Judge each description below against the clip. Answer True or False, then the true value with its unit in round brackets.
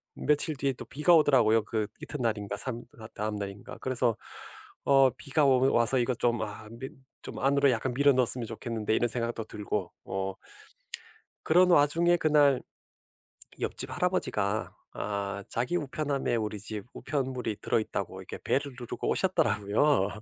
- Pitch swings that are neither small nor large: True (4.5 semitones)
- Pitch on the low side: True (125 Hz)